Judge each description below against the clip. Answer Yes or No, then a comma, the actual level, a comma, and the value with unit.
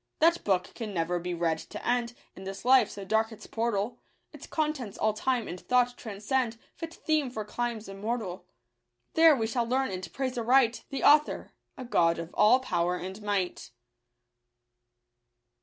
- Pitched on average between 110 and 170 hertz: No, high, 225 Hz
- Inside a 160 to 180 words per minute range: Yes, average, 175 wpm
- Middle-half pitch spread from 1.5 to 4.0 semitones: No, average, 4.7 semitones